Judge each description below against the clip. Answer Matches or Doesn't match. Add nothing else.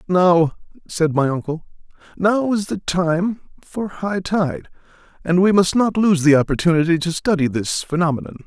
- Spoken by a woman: Doesn't match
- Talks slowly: Doesn't match